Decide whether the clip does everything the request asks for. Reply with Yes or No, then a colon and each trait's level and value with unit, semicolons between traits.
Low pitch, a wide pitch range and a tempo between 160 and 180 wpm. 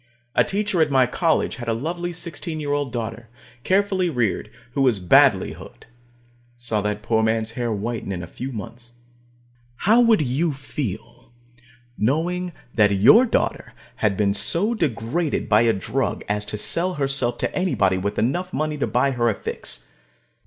Yes: low, 125 Hz; wide, 7.0 semitones; average, 170 wpm